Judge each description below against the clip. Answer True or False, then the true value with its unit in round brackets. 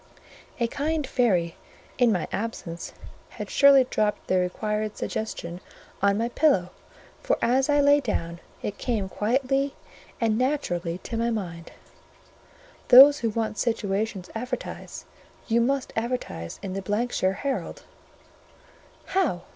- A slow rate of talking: True (125 wpm)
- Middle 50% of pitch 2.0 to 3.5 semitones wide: False (5.4 semitones)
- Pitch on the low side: False (225 Hz)